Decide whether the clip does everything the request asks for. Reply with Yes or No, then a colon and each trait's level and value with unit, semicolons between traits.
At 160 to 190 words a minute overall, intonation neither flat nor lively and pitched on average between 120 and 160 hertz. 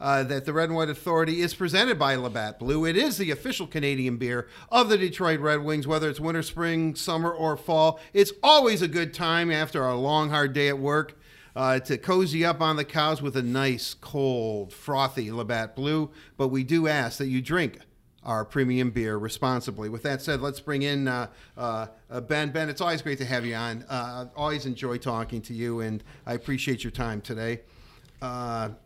No: fast, 205 wpm; average, 4.4 semitones; medium, 140 Hz